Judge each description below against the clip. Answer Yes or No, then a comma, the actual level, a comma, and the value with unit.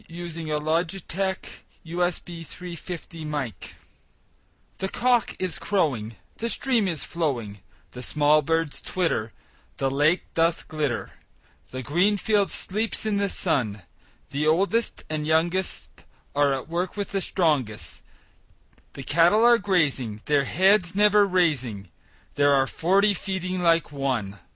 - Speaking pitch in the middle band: Yes, medium, 165 Hz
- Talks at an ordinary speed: No, slow, 125 wpm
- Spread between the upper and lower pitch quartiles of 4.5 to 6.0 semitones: Yes, average, 4.9 semitones